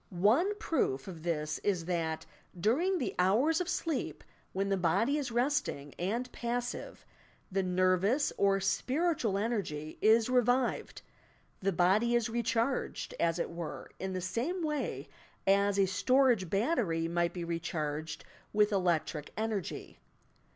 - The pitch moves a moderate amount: No, wide, 6.1 semitones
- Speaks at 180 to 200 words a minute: No, slow, 135 wpm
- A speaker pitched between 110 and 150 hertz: No, high, 200 Hz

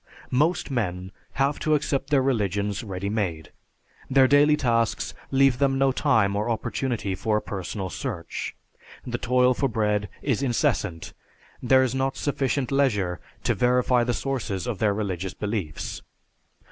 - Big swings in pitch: No, average, 4.9 semitones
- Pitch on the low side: Yes, low, 120 Hz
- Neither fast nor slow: Yes, average, 145 wpm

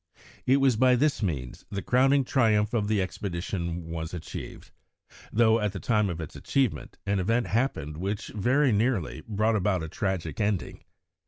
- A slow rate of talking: No, average, 165 wpm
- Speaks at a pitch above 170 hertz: No, low, 105 Hz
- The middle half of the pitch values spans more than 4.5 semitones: Yes, average, 4.9 semitones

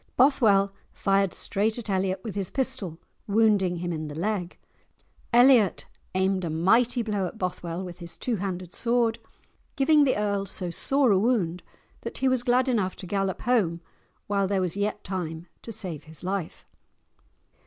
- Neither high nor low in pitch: No, high, 195 Hz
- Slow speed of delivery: No, average, 165 wpm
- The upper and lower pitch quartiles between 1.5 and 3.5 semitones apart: No, average, 4.2 semitones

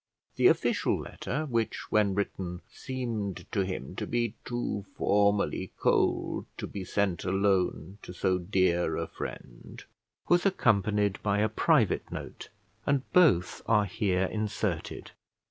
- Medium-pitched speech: No, low, 100 Hz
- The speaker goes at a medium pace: No, slow, 130 wpm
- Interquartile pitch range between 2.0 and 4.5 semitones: Yes, average, 3.5 semitones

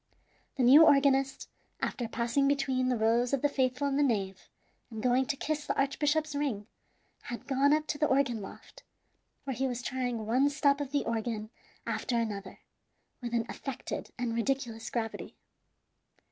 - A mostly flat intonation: No, average, 3.2 semitones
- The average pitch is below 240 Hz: No, very high, 255 Hz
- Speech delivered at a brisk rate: No, average, 165 wpm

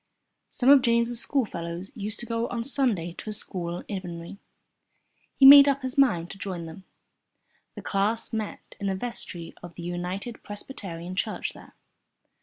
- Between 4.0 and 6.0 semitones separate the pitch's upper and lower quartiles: Yes, average, 5.3 semitones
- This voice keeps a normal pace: Yes, average, 165 wpm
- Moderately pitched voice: No, high, 200 Hz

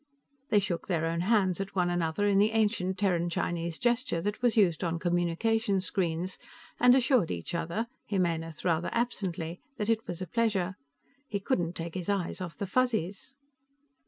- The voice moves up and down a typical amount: Yes, average, 3.8 semitones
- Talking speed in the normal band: Yes, average, 170 wpm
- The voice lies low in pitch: No, medium, 185 Hz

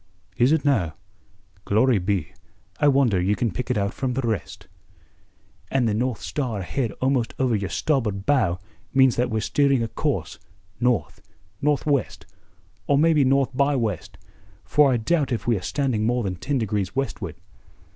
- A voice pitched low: Yes, low, 125 Hz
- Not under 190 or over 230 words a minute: No, average, 165 wpm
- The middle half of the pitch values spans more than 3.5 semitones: Yes, average, 4.6 semitones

